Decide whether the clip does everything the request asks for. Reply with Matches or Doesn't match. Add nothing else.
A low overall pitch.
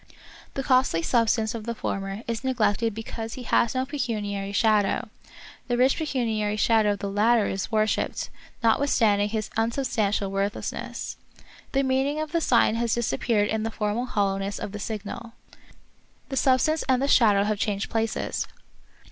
Doesn't match